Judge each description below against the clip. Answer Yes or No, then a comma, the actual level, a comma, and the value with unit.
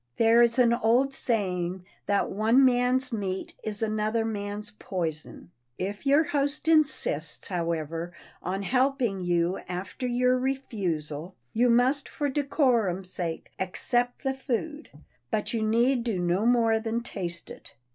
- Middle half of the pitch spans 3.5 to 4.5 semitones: No, average, 5.3 semitones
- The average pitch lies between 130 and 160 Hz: No, high, 225 Hz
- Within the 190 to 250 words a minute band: No, slow, 135 wpm